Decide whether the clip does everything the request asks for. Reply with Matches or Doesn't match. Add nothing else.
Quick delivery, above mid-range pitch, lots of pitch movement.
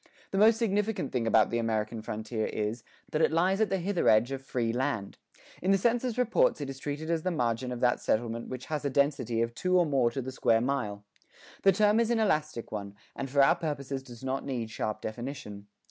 Doesn't match